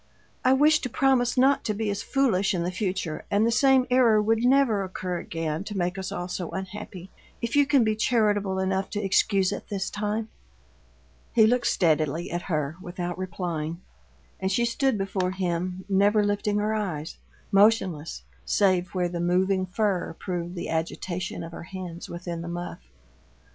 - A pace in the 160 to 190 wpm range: Yes, average, 175 wpm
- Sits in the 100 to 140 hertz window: No, high, 190 Hz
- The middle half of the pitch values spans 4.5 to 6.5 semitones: No, average, 3.6 semitones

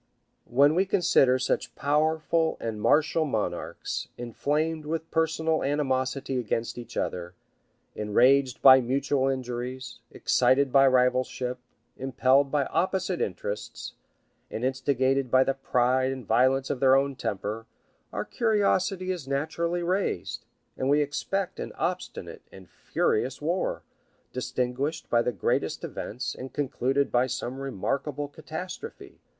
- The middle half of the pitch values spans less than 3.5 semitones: No, average, 3.8 semitones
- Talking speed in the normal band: No, slow, 125 wpm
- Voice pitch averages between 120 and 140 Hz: Yes, low, 135 Hz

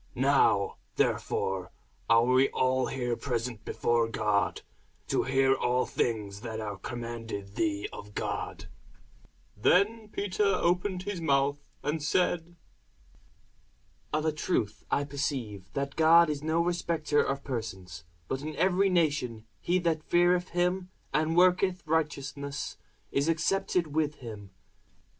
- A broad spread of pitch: Yes, wide, 6.5 semitones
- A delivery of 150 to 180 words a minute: No, slow, 135 wpm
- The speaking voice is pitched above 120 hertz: Yes, medium, 140 Hz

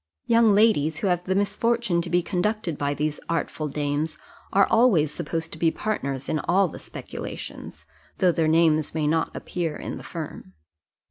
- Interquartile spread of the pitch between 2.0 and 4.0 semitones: No, average, 4.5 semitones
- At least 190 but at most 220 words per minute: No, average, 175 wpm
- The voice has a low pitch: No, medium, 165 Hz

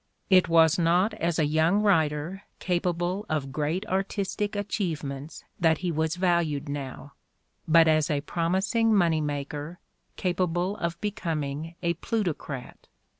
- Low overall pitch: No, medium, 165 Hz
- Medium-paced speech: No, slow, 125 wpm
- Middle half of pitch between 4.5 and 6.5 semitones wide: No, average, 3.4 semitones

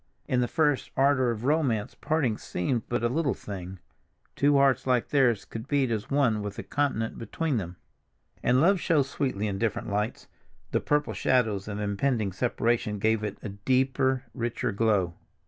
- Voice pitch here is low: Yes, low, 120 Hz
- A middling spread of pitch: Yes, average, 4.6 semitones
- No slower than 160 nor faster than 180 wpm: Yes, average, 165 wpm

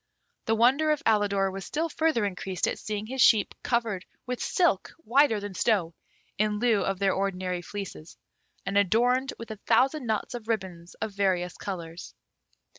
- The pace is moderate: Yes, average, 165 wpm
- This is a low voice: No, high, 210 Hz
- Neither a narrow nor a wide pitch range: Yes, average, 4.0 semitones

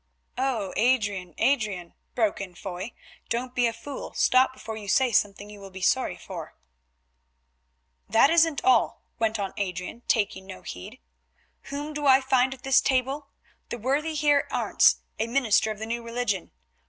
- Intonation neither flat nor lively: Yes, average, 4.5 semitones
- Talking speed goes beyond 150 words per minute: Yes, average, 165 wpm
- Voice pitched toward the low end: No, high, 235 Hz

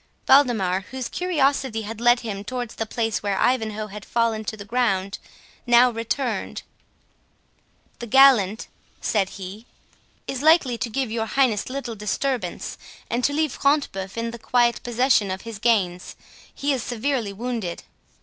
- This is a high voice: Yes, high, 230 Hz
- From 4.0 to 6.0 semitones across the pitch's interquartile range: No, average, 3.5 semitones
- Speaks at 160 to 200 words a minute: No, average, 150 wpm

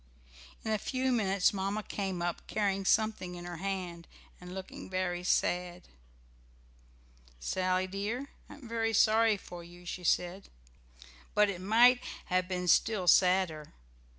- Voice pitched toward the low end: No, high, 190 Hz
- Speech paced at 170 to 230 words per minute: No, average, 140 wpm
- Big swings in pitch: No, average, 3.1 semitones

